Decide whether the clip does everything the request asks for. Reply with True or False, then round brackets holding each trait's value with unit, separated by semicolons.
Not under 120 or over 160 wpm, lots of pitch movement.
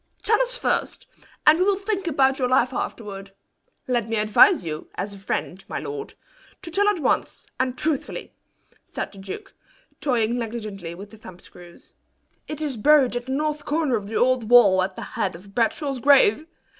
False (185 wpm; 7.0 semitones)